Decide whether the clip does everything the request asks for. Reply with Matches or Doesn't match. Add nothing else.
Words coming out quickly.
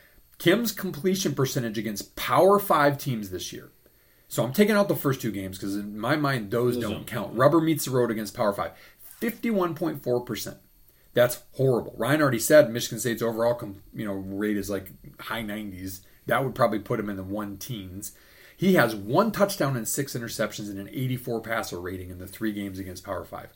Doesn't match